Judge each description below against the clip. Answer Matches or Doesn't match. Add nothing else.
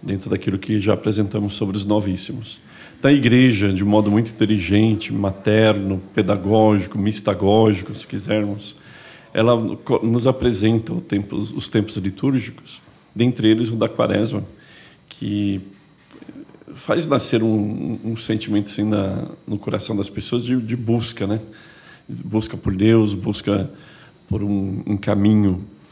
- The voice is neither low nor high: Doesn't match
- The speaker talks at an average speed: Matches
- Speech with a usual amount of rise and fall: Doesn't match